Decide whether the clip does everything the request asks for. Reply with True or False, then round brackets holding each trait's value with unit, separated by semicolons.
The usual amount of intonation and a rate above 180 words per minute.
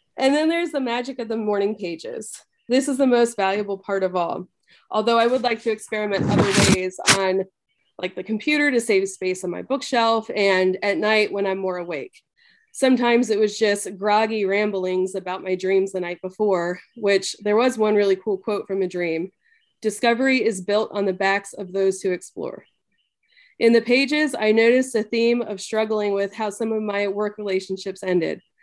True (3.7 semitones; 190 wpm)